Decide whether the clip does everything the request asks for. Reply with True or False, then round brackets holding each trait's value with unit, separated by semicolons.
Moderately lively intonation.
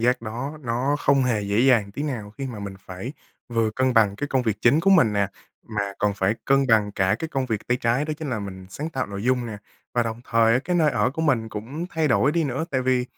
True (4.5 semitones)